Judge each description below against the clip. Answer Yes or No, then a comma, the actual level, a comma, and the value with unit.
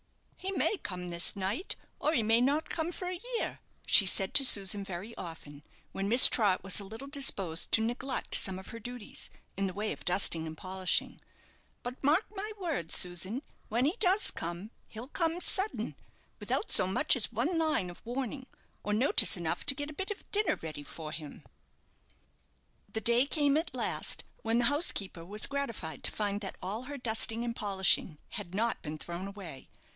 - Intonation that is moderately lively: No, wide, 7.0 semitones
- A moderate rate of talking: Yes, average, 190 wpm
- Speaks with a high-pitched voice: Yes, high, 220 Hz